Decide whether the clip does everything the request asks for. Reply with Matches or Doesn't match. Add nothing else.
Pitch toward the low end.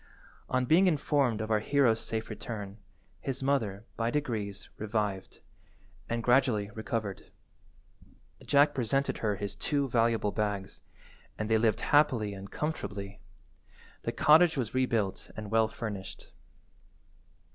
Matches